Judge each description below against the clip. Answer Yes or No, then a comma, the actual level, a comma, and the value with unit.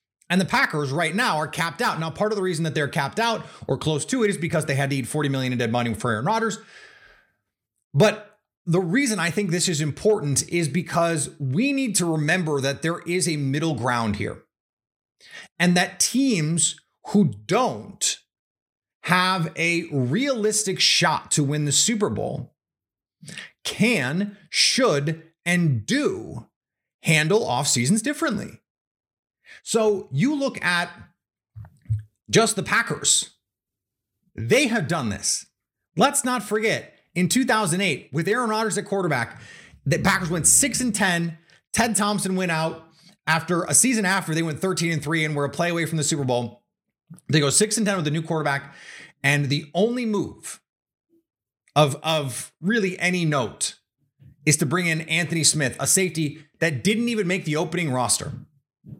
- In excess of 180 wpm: No, average, 165 wpm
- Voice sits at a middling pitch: Yes, medium, 170 Hz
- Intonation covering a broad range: Yes, wide, 5.9 semitones